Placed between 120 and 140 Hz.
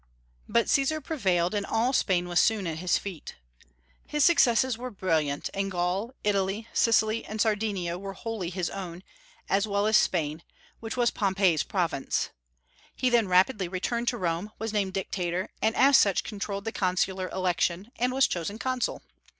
No: high, 200 Hz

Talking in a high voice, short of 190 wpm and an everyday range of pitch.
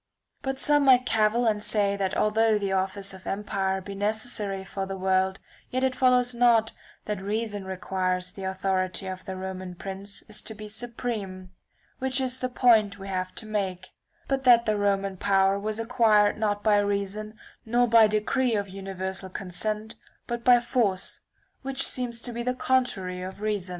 Yes: high, 205 Hz; average, 175 wpm; average, 3.5 semitones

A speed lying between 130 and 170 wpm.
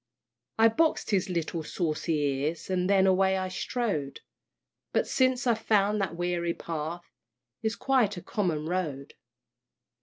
Yes: average, 140 wpm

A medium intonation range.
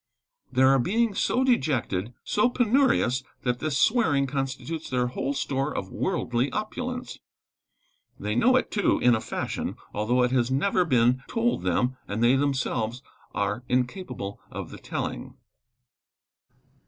No: wide, 8.2 semitones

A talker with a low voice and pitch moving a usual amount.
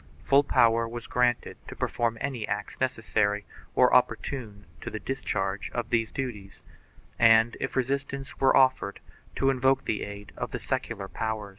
Yes: low, 115 Hz; average, 4.0 semitones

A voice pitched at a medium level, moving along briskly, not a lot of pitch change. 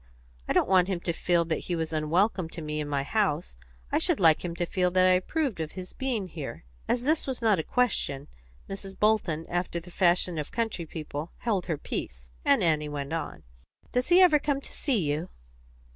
No: medium, 175 Hz; fast, 215 wpm; average, 5.0 semitones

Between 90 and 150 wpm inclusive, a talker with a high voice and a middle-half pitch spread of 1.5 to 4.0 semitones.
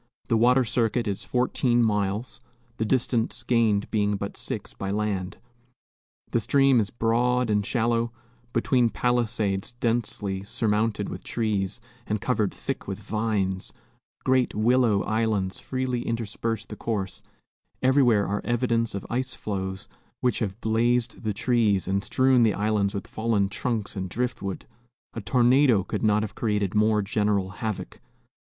No: average, 140 wpm; low, 110 Hz; average, 2.8 semitones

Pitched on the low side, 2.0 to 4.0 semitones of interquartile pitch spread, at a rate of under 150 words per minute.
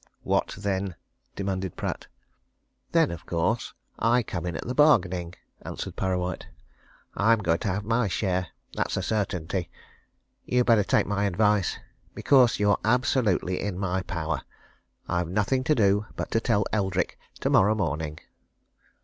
Yes: low, 100 Hz; average, 3.5 semitones; average, 140 wpm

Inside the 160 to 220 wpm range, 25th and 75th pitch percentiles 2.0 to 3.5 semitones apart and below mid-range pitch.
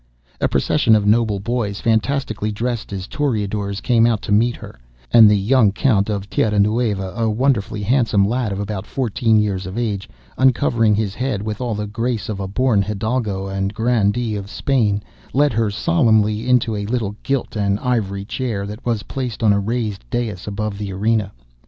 Yes: average, 185 wpm; average, 2.8 semitones; low, 110 Hz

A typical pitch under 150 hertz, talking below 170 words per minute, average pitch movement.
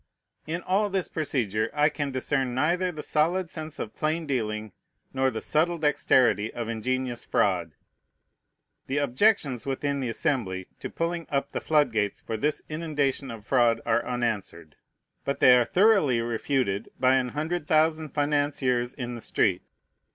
Yes: low, 135 Hz; average, 155 wpm; average, 4.7 semitones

